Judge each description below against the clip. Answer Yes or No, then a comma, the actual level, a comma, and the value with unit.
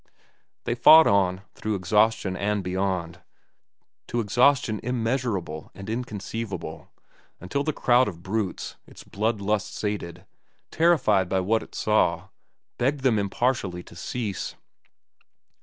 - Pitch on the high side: No, low, 105 Hz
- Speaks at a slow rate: Yes, slow, 120 wpm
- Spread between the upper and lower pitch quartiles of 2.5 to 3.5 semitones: No, average, 4.2 semitones